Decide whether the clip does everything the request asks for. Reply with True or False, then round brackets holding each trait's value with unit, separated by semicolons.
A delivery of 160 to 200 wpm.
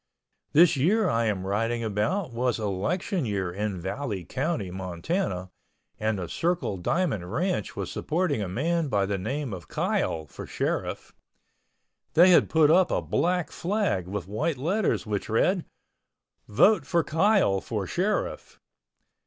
False (145 wpm)